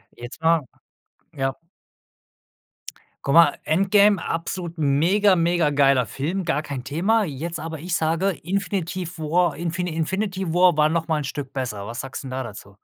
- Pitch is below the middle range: No, medium, 165 Hz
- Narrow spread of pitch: No, average, 4.1 semitones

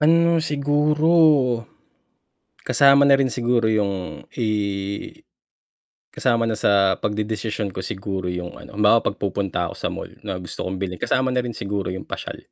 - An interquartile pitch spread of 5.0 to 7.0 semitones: Yes, wide, 5.6 semitones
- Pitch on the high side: No, low, 110 Hz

